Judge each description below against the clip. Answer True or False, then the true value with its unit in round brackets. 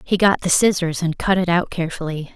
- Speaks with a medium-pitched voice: True (175 Hz)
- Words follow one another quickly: True (230 wpm)